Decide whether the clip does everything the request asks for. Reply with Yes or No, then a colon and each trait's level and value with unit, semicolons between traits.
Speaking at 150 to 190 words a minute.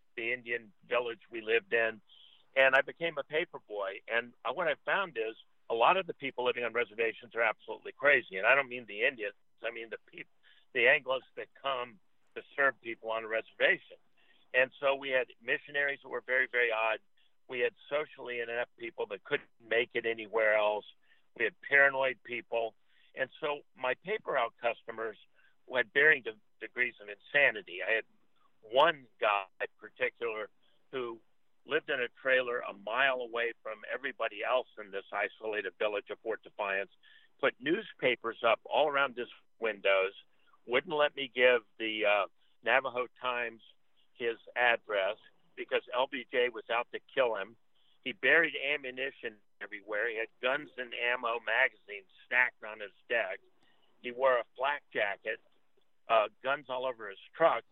Yes: average, 165 wpm